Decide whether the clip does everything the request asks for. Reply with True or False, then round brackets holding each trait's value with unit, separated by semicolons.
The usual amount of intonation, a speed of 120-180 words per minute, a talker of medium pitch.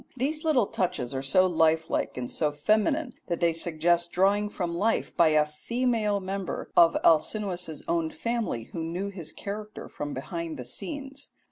True (4.9 semitones; 160 wpm; 175 Hz)